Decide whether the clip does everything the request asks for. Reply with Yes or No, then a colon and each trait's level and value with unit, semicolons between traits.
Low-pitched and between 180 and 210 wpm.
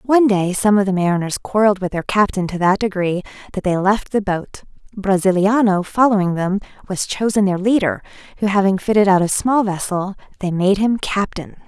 No: high, 195 Hz; average, 185 wpm